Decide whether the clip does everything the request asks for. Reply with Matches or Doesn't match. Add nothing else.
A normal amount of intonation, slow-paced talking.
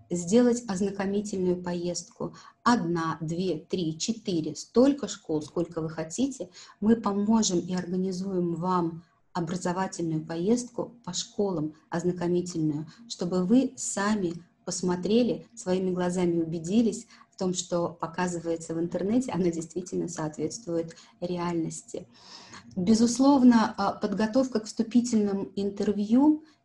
Matches